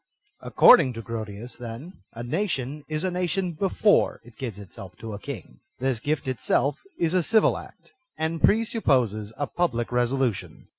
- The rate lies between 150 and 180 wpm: Yes, average, 160 wpm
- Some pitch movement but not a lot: No, wide, 6.5 semitones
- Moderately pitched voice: No, low, 130 Hz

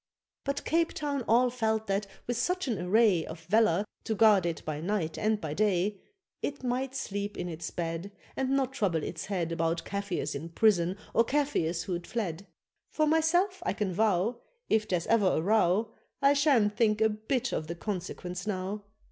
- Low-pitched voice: No, high, 210 Hz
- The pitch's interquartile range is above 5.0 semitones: Yes, wide, 5.5 semitones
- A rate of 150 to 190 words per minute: Yes, average, 180 wpm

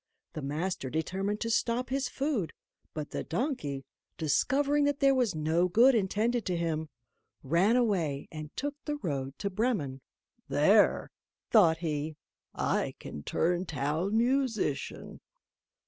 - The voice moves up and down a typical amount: No, wide, 7.8 semitones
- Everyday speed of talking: No, slow, 130 wpm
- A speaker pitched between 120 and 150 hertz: No, medium, 185 Hz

